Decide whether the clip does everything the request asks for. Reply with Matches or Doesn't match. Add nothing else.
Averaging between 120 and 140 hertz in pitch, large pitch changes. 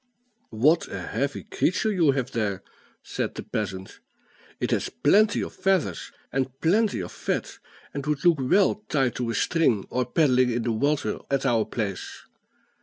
Matches